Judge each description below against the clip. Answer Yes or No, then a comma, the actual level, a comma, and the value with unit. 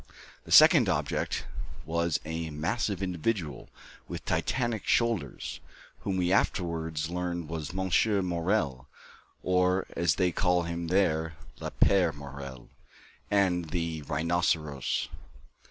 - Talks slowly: Yes, slow, 110 wpm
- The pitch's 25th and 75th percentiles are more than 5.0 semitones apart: No, average, 2.7 semitones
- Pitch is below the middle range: Yes, very low, 85 Hz